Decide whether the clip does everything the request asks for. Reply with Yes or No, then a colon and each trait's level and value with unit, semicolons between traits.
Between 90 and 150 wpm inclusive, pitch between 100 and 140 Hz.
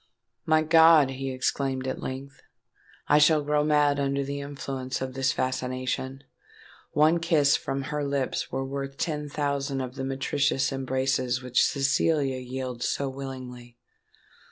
Yes: average, 140 wpm; low, 135 Hz